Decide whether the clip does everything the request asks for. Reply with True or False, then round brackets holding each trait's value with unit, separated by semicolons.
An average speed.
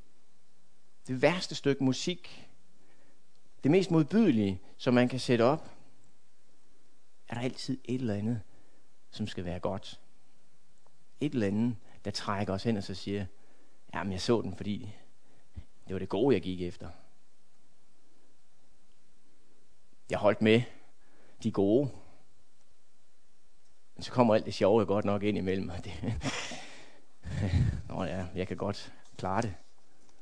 False (135 wpm)